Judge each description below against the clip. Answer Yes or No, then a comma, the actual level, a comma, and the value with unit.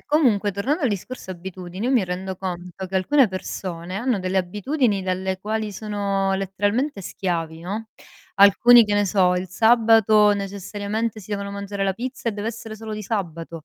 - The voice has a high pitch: Yes, high, 200 Hz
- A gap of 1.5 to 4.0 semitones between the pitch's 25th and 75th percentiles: Yes, average, 2.8 semitones